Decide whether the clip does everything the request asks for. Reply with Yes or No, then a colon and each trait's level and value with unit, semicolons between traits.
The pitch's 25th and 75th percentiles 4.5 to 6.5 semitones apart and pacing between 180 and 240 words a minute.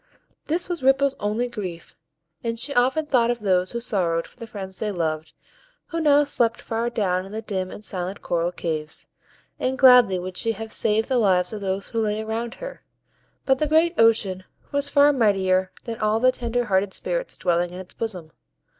Yes: average, 4.9 semitones; average, 195 wpm